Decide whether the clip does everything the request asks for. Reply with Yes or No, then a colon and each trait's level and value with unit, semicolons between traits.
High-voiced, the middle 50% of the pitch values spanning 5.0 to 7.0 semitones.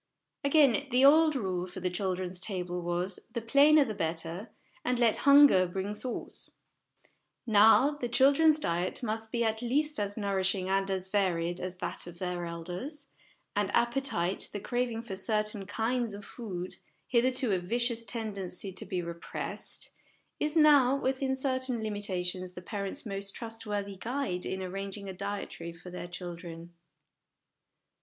Yes: high, 205 Hz; average, 5.3 semitones